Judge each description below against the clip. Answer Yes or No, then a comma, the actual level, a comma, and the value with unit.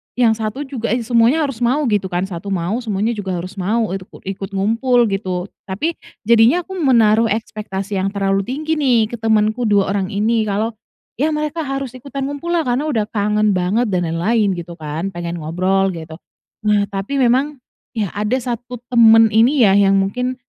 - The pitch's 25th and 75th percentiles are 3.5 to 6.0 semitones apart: Yes, average, 4.2 semitones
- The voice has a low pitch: No, high, 215 Hz